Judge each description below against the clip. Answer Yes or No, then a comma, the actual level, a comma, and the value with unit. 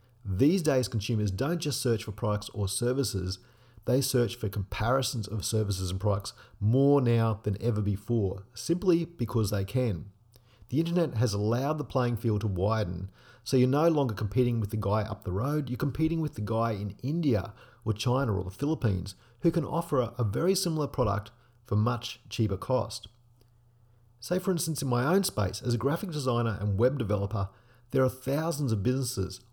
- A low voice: Yes, low, 120 Hz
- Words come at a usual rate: Yes, average, 180 wpm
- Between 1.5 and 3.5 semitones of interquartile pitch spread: No, average, 4.0 semitones